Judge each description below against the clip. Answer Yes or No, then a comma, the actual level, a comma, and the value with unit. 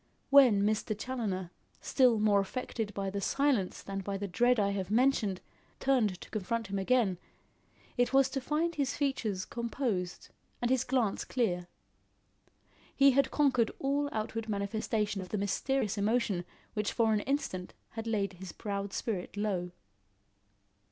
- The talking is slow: No, average, 150 wpm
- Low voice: No, high, 215 Hz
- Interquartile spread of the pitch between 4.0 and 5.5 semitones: Yes, average, 4.3 semitones